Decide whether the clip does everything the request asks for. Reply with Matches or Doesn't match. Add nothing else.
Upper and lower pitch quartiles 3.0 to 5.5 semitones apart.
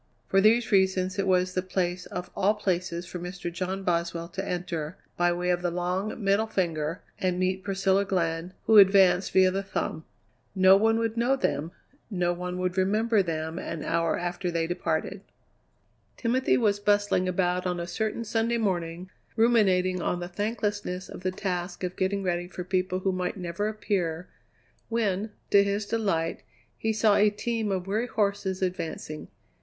Doesn't match